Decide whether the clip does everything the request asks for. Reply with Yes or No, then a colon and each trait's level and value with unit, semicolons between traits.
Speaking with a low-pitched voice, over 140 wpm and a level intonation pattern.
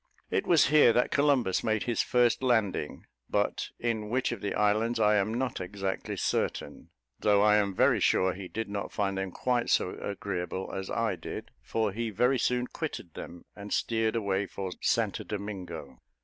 No: low, 105 Hz; average, 175 wpm; average, 3.5 semitones